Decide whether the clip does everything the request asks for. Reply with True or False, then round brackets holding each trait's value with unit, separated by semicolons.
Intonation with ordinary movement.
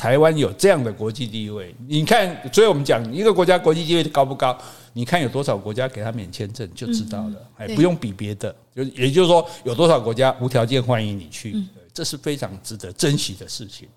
False (5.9 semitones)